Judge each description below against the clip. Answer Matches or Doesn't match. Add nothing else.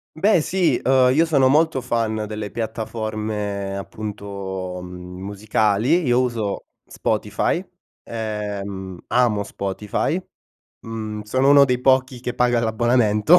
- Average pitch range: Matches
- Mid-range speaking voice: Doesn't match